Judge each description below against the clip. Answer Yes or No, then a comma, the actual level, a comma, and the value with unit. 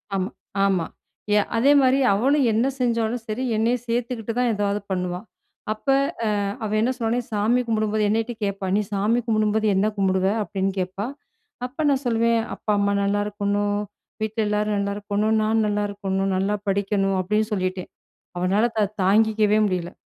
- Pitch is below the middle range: No, high, 210 Hz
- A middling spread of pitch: No, narrow, 2.3 semitones